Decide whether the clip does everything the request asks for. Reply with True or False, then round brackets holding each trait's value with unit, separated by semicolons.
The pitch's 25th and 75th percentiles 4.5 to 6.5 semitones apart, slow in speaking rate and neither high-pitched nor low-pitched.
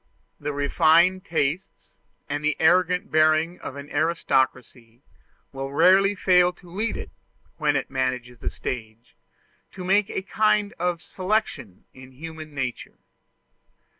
True (5.2 semitones; 130 wpm; 155 Hz)